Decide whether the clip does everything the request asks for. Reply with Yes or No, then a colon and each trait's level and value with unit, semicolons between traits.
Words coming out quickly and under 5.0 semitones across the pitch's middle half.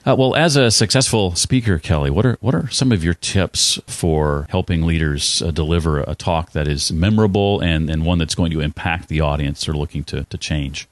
No: fast, 215 wpm; wide, 5.5 semitones